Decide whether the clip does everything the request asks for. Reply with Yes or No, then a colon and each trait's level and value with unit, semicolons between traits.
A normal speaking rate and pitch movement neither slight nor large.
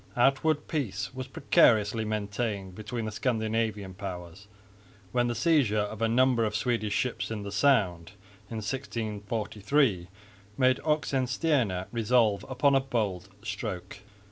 No: slow, 125 wpm; average, 3.9 semitones